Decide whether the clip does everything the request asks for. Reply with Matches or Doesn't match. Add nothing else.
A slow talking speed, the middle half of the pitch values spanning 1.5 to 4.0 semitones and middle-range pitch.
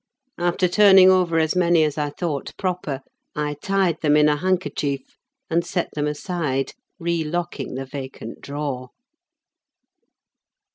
Matches